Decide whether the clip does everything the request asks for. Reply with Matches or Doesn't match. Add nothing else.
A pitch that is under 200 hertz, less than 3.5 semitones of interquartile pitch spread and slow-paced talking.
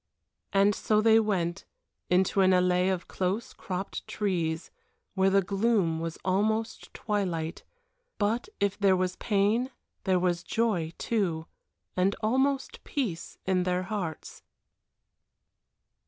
Matches